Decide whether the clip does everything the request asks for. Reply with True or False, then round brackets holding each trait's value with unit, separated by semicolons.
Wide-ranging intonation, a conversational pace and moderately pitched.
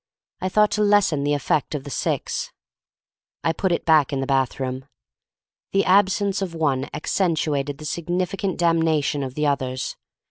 False (4.8 semitones; 155 wpm; 155 Hz)